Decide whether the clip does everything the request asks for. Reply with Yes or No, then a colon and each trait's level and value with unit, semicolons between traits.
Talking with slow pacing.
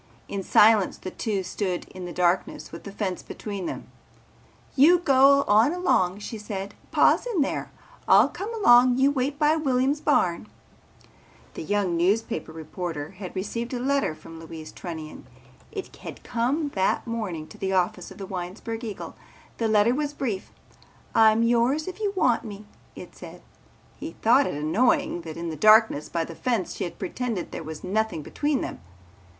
No: average, 170 wpm